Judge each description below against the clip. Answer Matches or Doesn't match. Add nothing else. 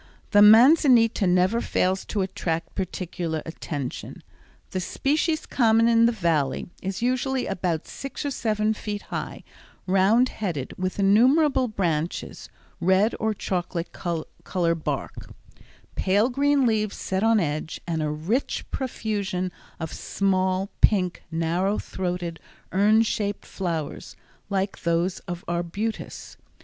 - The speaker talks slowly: Matches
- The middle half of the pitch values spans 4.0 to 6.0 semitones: Matches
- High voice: Matches